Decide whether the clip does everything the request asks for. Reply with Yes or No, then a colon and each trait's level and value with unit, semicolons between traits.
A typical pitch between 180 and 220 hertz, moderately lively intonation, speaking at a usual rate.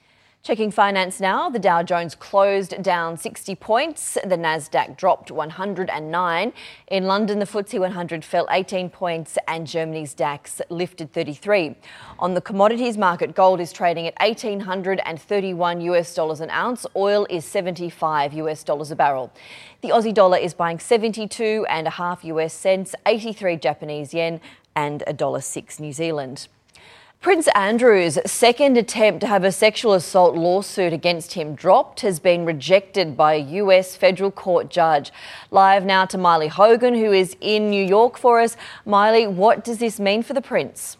Yes: medium, 185 Hz; average, 3.7 semitones; average, 155 wpm